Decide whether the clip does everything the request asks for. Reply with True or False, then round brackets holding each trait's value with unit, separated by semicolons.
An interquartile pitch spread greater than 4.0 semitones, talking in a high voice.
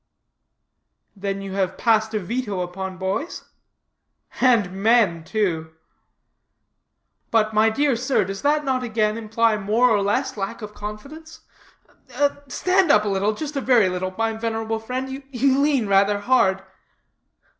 True (4.4 semitones; 220 Hz)